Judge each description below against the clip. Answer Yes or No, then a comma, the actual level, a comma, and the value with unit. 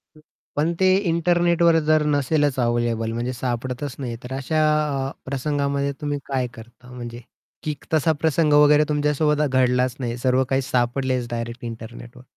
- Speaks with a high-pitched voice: No, low, 135 Hz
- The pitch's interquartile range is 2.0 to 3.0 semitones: No, average, 3.4 semitones